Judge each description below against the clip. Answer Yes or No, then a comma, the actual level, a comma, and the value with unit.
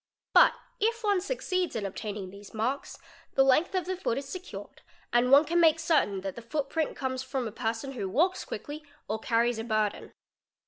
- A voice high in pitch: Yes, very high, 265 Hz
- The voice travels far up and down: Yes, wide, 6.8 semitones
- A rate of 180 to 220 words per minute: Yes, average, 190 wpm